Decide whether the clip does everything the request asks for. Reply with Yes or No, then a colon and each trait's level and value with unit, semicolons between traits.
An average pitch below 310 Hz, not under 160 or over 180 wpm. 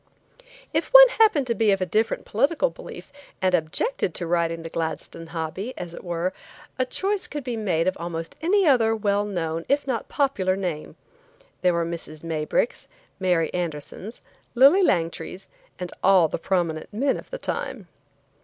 Yes: medium, 185 Hz; average, 165 wpm